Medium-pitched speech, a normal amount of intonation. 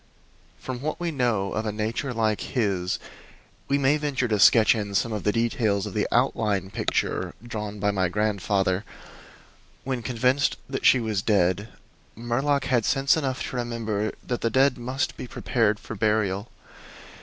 No: low, 115 Hz; average, 3.8 semitones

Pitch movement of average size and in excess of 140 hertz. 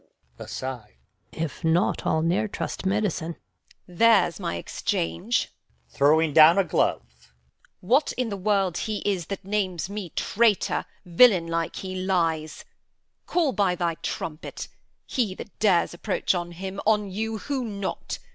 Yes: average, 4.1 semitones; medium, 185 Hz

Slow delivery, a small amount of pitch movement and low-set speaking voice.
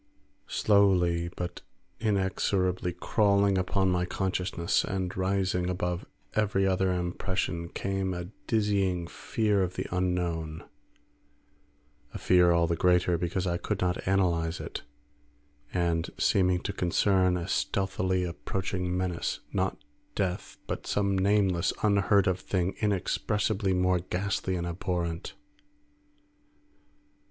Yes: slow, 115 wpm; narrow, 1.7 semitones; very low, 90 Hz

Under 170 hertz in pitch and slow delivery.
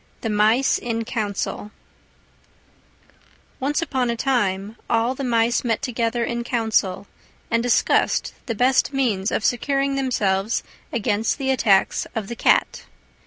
No: high, 235 Hz; slow, 130 wpm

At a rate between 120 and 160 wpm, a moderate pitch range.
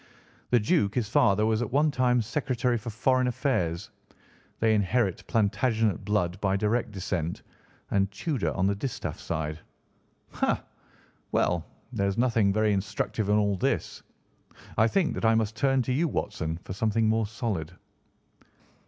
Yes: average, 155 wpm; average, 3.6 semitones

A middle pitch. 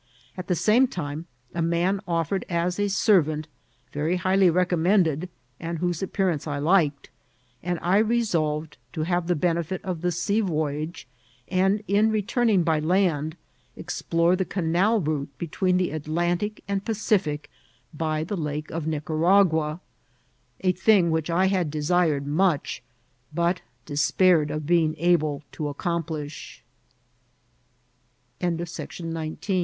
Yes: medium, 170 Hz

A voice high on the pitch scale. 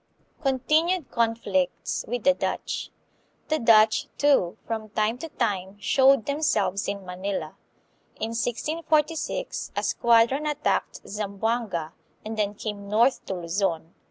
Yes: high, 225 Hz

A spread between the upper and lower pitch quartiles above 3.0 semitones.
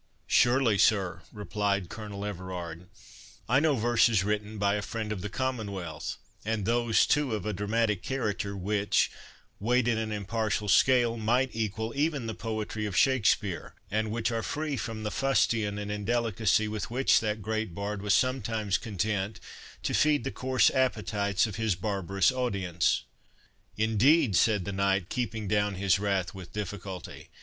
No: narrow, 2.6 semitones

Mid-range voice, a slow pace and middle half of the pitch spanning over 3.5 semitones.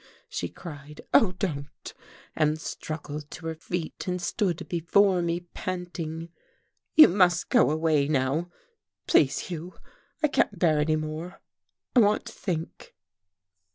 No: medium, 165 Hz; slow, 130 wpm; average, 2.7 semitones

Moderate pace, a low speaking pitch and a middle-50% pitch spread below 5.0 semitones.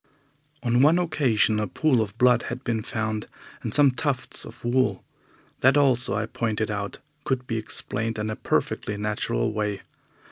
Yes: average, 165 wpm; low, 115 Hz; average, 3.2 semitones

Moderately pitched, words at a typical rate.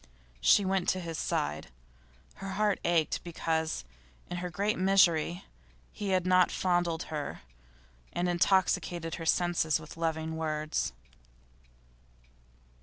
No: medium, 175 Hz; slow, 115 wpm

